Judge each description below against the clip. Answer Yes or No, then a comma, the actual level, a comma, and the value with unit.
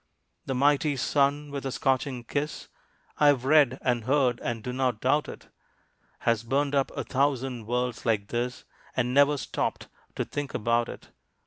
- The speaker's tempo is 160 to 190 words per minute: Yes, average, 165 wpm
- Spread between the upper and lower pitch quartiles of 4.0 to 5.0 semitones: No, average, 2.9 semitones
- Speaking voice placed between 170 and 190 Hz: No, low, 130 Hz